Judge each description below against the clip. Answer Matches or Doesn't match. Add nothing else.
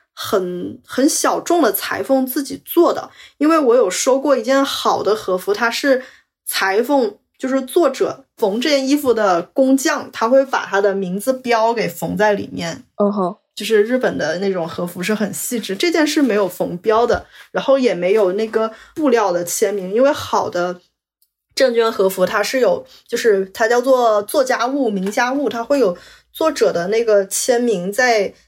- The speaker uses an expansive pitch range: Doesn't match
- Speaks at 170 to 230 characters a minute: Doesn't match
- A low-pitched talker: Doesn't match